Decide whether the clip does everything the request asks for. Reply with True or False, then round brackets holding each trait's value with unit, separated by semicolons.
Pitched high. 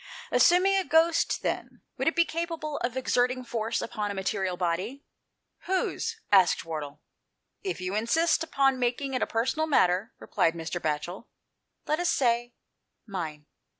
True (240 Hz)